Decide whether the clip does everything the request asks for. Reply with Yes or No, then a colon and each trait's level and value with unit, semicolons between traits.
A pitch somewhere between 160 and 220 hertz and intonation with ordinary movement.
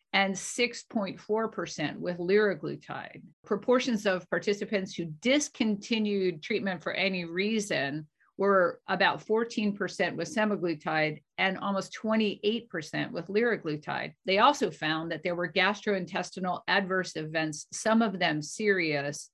Yes: high, 190 Hz; average, 3.8 semitones